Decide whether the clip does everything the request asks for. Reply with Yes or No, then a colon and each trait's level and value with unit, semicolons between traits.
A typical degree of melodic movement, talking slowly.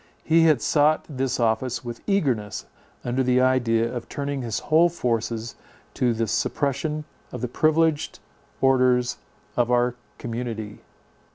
Yes: average, 3.7 semitones; slow, 130 wpm